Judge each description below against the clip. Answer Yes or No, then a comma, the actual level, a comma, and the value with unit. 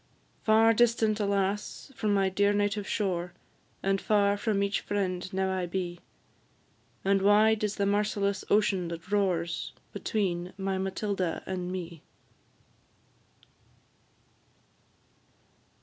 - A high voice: Yes, high, 200 Hz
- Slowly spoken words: Yes, slow, 110 wpm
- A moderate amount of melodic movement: No, narrow, 1.9 semitones